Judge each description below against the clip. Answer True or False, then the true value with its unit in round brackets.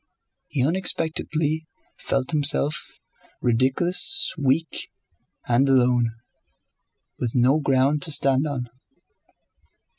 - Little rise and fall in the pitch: False (3.4 semitones)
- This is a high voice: False (140 Hz)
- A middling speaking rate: False (85 wpm)